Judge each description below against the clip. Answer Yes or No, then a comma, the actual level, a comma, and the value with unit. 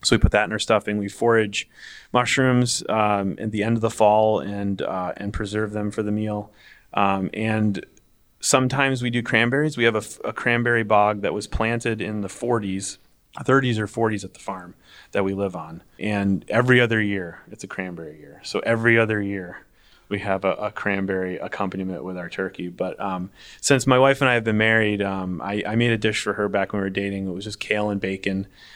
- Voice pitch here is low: Yes, low, 105 Hz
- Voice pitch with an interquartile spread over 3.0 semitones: No, average, 2.7 semitones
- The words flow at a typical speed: No, fast, 215 wpm